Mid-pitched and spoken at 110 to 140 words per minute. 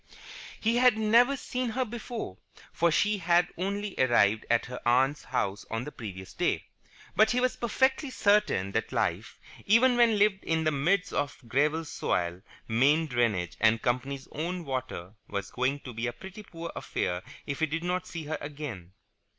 No: medium, 155 Hz; average, 175 wpm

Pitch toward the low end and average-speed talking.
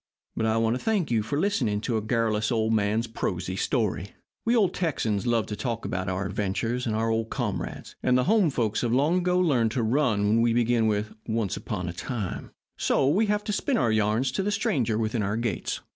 No: low, 115 Hz; fast, 220 wpm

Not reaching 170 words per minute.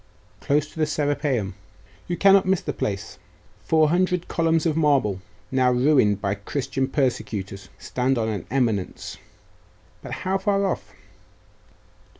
Yes: average, 140 wpm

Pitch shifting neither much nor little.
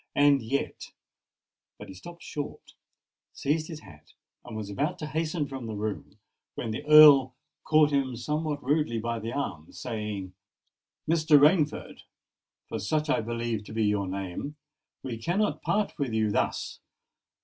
No: wide, 5.8 semitones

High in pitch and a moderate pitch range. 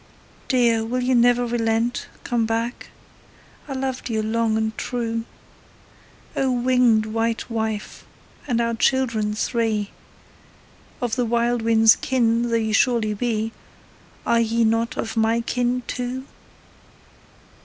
No: high, 230 Hz; narrow, 1.6 semitones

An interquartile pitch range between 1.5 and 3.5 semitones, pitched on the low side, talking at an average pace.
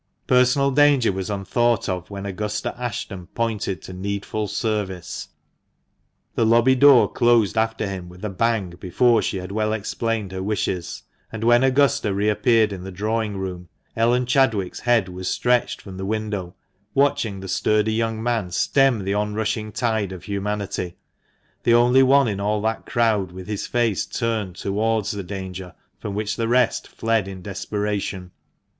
Yes: average, 3.2 semitones; low, 105 Hz; average, 165 wpm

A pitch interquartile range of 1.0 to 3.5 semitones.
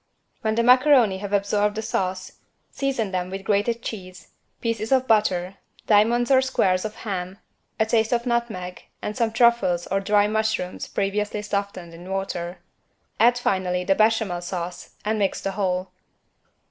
Yes: average, 3.2 semitones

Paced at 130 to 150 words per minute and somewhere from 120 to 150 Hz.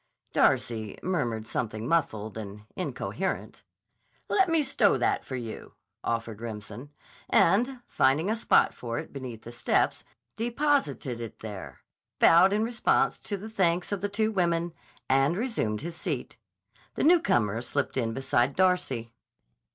Yes: average, 140 wpm; medium, 140 Hz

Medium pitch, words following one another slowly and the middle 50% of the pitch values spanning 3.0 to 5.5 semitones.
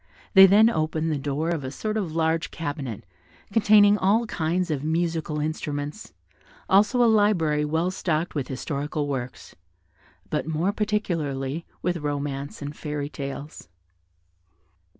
Yes: medium, 160 Hz; slow, 130 wpm; average, 4.5 semitones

